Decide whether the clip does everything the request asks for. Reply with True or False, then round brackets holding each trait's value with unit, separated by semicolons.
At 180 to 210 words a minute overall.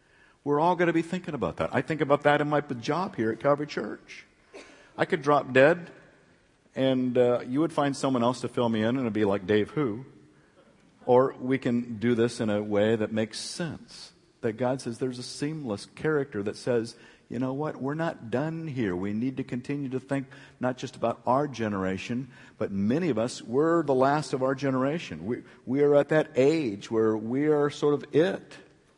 True (205 wpm)